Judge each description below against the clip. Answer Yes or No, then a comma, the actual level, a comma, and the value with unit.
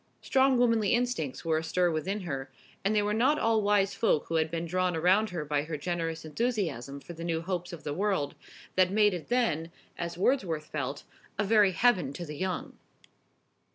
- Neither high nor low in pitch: Yes, medium, 180 Hz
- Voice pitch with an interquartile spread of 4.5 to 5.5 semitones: Yes, average, 4.8 semitones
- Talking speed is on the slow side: No, average, 190 wpm